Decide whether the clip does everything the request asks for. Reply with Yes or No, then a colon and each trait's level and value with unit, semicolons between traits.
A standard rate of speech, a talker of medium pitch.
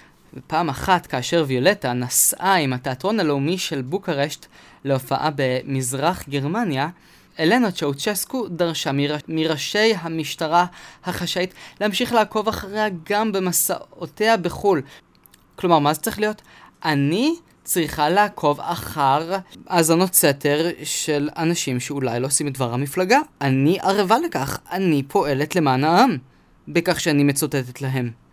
Yes: average, 120 wpm; medium, 160 Hz